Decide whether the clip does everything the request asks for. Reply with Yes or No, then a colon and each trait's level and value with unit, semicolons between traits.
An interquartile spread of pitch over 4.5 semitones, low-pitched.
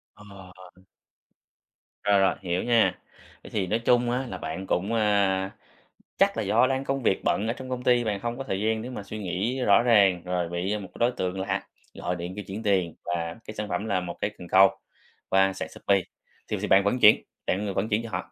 No: average, 3.4 semitones; low, 100 Hz